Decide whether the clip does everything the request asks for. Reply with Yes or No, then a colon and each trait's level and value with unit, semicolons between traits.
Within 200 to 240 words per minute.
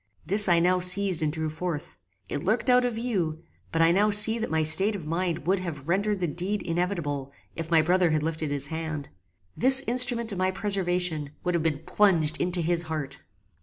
Yes: fast, 205 wpm